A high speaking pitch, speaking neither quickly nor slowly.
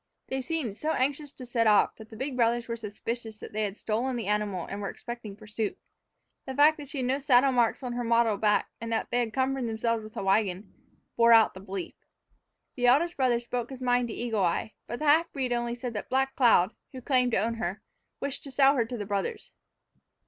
No: high, 235 Hz; fast, 230 wpm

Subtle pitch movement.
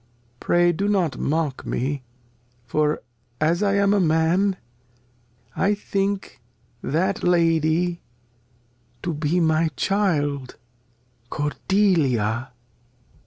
No: average, 4.4 semitones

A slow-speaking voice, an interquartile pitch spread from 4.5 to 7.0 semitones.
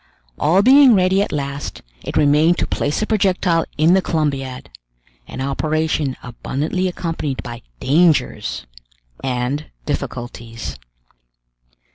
Yes: slow, 110 wpm; average, 5.0 semitones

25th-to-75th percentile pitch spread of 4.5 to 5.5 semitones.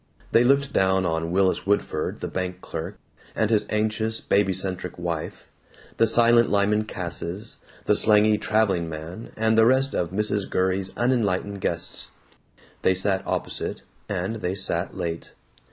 No: average, 3.2 semitones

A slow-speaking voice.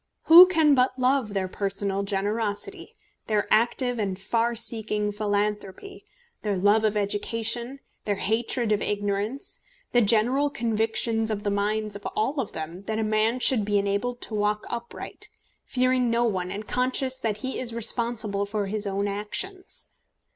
No: average, 155 wpm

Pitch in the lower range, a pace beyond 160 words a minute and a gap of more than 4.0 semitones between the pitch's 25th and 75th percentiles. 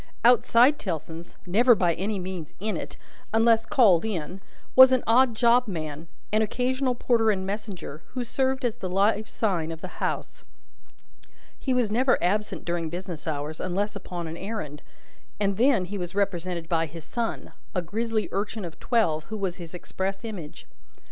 No: high, 200 Hz; average, 170 wpm; average, 4.8 semitones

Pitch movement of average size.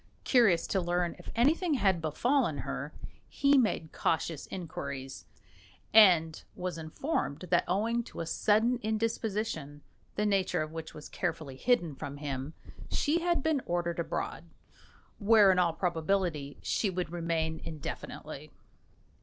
No: wide, 5.7 semitones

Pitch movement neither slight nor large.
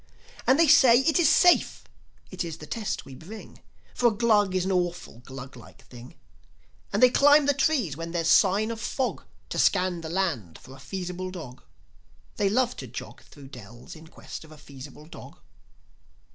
No: wide, 7.9 semitones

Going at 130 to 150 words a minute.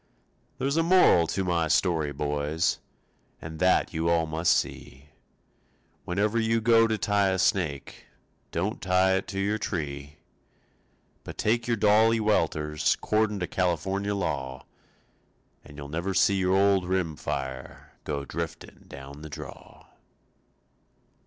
Yes: slow, 135 wpm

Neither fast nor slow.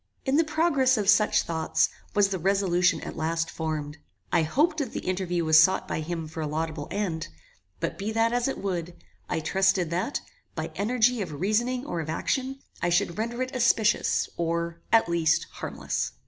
Yes: average, 185 wpm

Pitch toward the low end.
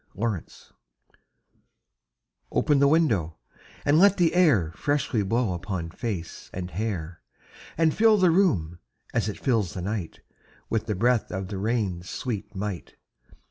Yes: low, 110 Hz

